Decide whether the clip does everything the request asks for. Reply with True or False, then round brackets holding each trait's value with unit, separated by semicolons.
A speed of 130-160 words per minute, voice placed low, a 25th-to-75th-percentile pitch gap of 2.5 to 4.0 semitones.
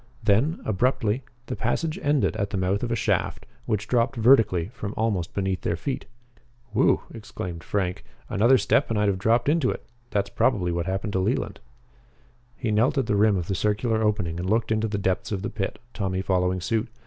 False (195 wpm; 105 Hz; 3.4 semitones)